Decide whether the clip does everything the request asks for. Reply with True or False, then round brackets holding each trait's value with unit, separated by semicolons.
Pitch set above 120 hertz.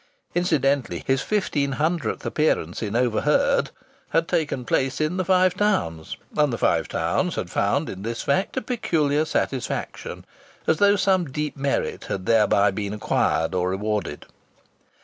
True (140 Hz)